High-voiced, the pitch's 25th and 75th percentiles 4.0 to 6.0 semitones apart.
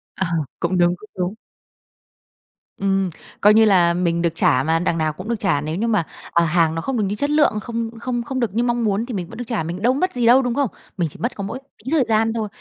Yes: high, 210 Hz; wide, 5.4 semitones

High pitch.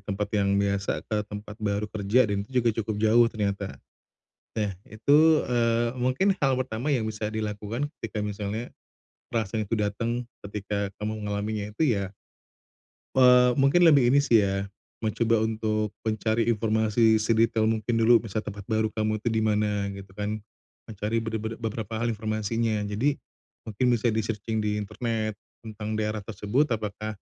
No: low, 110 Hz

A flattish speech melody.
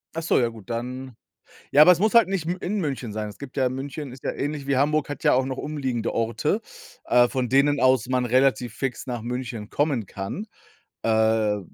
No: average, 3.7 semitones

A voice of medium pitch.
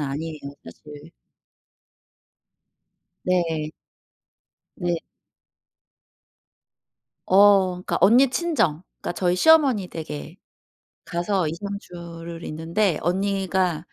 Yes: medium, 175 Hz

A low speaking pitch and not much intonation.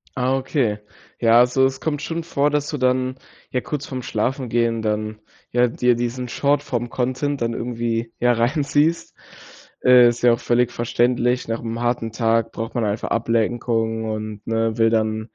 Yes: low, 120 Hz; narrow, 2.2 semitones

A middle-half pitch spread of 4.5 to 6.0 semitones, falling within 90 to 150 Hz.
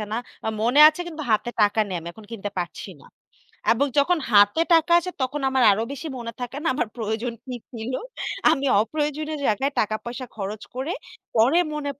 No: average, 5.2 semitones; high, 245 Hz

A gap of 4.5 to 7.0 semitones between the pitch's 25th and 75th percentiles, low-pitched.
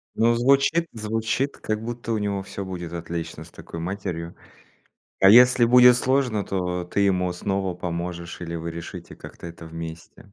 Yes: average, 5.2 semitones; very low, 95 Hz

